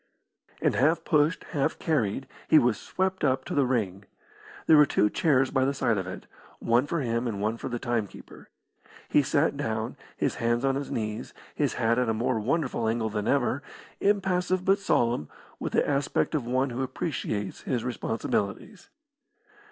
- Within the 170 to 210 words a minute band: Yes, average, 175 wpm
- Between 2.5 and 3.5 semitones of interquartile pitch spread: No, average, 4.5 semitones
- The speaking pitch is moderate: No, low, 125 Hz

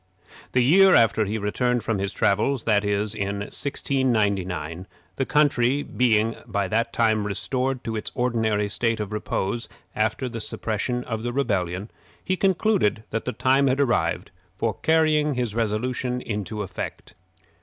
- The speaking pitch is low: Yes, low, 115 Hz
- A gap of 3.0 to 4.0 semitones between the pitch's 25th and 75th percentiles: Yes, average, 3.7 semitones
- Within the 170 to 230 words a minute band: No, average, 150 wpm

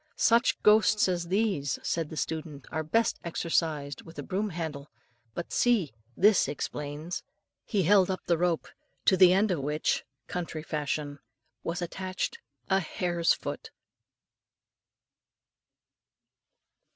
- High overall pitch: No, medium, 170 Hz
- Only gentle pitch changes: No, average, 3.8 semitones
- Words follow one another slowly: Yes, slow, 125 wpm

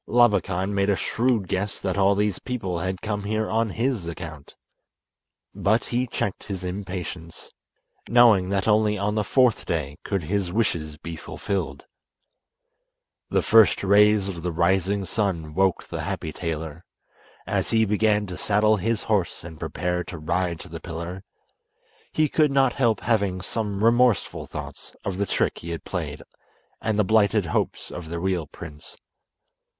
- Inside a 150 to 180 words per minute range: Yes, average, 160 wpm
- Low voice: Yes, low, 100 Hz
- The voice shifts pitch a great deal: No, average, 3.6 semitones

